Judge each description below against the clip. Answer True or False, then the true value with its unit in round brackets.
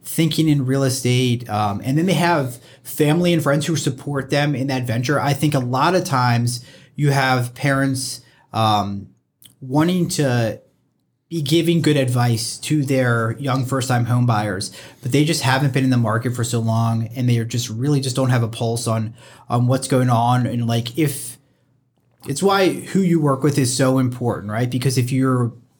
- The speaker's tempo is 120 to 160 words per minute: False (190 wpm)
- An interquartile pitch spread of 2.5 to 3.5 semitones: True (3.0 semitones)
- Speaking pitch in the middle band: False (130 Hz)